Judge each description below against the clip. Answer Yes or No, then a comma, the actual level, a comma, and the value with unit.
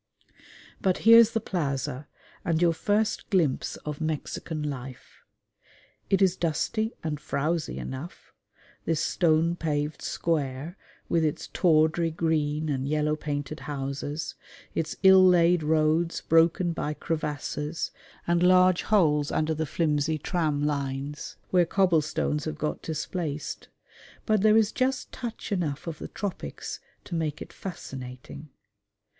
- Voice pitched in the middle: Yes, medium, 160 Hz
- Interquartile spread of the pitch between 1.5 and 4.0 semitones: Yes, average, 3.0 semitones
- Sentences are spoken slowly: Yes, slow, 130 wpm